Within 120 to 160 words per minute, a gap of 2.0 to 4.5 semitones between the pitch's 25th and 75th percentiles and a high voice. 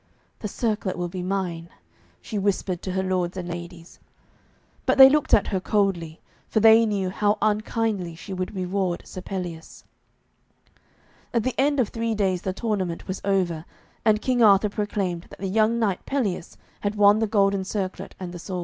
No: average, 175 wpm; average, 2.9 semitones; high, 195 Hz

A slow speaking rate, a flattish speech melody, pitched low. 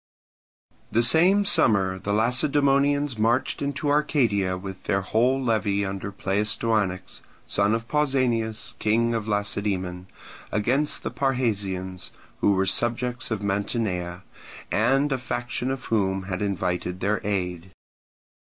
No: slow, 120 wpm; average, 4.5 semitones; low, 110 Hz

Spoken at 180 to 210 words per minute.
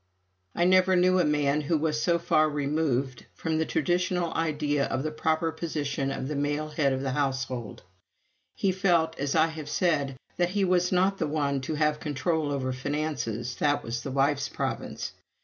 Yes: average, 185 wpm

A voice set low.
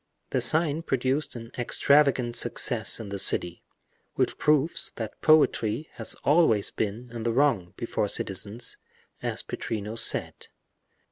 Yes: low, 120 Hz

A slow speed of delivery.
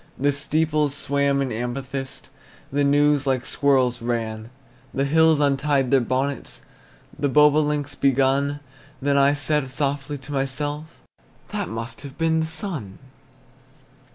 Yes: slow, 125 wpm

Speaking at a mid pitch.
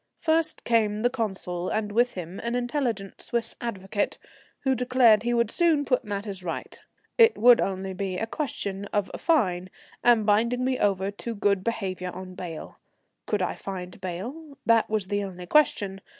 No: high, 210 Hz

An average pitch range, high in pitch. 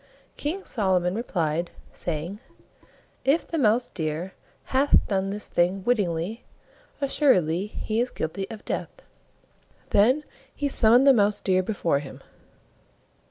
No: wide, 5.7 semitones; high, 205 Hz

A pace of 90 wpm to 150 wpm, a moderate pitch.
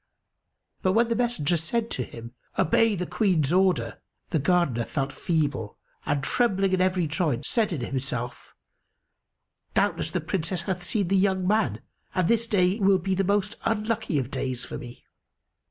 No: average, 165 wpm; medium, 180 Hz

